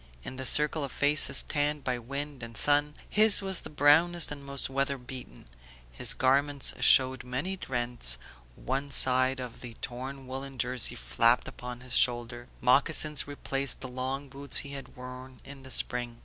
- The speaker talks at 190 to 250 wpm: No, average, 165 wpm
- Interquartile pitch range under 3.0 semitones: Yes, narrow, 2.4 semitones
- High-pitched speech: No, low, 135 Hz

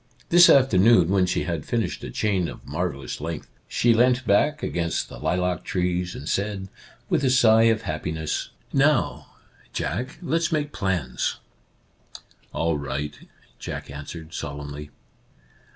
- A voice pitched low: Yes, very low, 90 Hz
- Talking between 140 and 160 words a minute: Yes, average, 145 wpm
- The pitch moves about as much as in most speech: No, wide, 7.0 semitones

